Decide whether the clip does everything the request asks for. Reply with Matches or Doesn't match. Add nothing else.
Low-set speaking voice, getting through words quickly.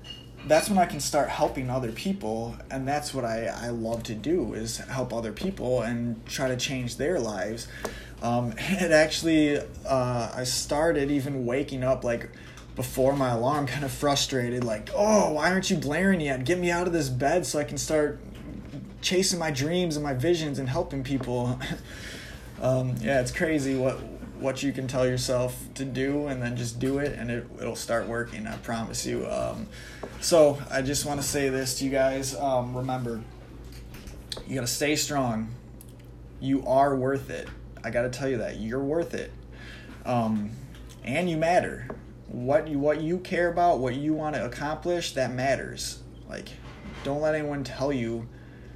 Doesn't match